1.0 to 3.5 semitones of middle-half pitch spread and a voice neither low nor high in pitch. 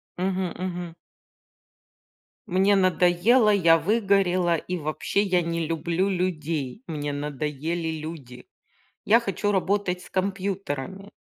Yes: average, 3.2 semitones; medium, 180 Hz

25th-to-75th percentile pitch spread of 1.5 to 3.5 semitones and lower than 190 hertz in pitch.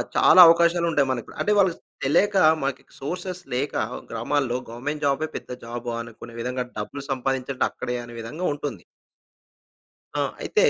No: average, 5.3 semitones; low, 135 Hz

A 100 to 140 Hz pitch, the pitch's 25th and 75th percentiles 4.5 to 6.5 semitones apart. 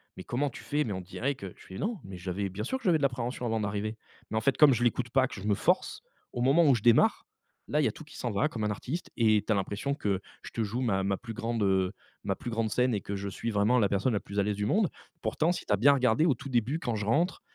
Yes: low, 115 Hz; average, 4.9 semitones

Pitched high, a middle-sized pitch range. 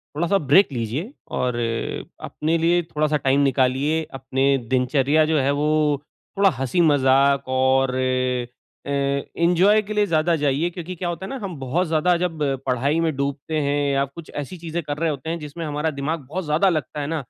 No: medium, 150 Hz; average, 3.4 semitones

